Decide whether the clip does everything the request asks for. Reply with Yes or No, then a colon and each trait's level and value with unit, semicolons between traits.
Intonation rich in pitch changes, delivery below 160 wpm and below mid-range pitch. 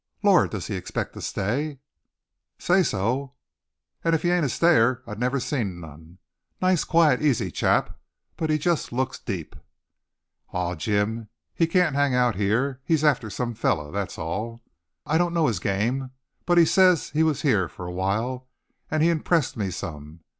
No: wide, 7.7 semitones; average, 175 wpm; low, 125 Hz